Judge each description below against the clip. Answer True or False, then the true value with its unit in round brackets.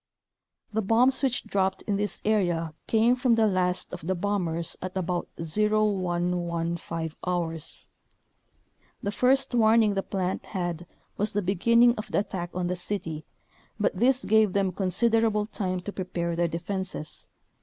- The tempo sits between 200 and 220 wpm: False (155 wpm)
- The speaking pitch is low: False (190 Hz)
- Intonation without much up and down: False (3.6 semitones)